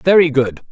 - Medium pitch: Yes, medium, 150 Hz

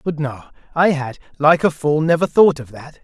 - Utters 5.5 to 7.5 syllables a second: No, 5.0 syllables/s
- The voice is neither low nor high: Yes, medium, 150 Hz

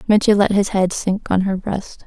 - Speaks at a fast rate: Yes, fast, 235 wpm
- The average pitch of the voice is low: No, high, 195 Hz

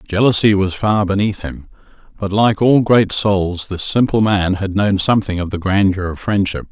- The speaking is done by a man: Yes, male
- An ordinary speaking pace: Yes, average, 190 wpm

